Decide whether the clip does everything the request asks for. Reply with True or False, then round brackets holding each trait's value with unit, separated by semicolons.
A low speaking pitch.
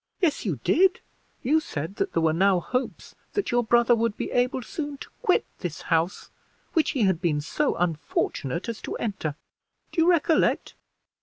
False (230 Hz)